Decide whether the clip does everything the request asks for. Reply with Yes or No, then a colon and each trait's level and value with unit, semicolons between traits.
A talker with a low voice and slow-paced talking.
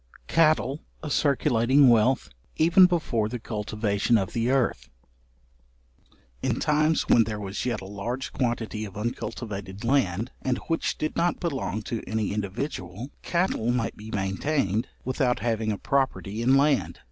No: low, 120 Hz; average, 145 wpm